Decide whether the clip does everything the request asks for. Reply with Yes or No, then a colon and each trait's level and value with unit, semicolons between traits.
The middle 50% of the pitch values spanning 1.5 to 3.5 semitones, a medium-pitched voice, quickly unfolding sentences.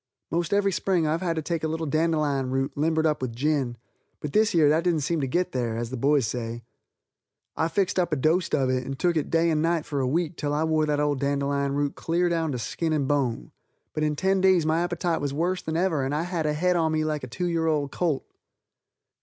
Yes: average, 3.1 semitones; medium, 155 Hz; fast, 250 wpm